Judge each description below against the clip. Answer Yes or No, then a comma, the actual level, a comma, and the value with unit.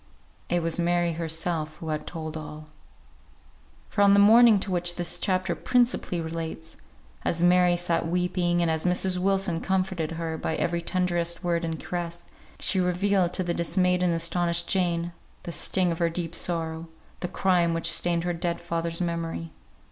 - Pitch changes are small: Yes, narrow, 1.4 semitones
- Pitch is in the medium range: Yes, medium, 175 Hz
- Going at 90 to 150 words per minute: No, average, 170 wpm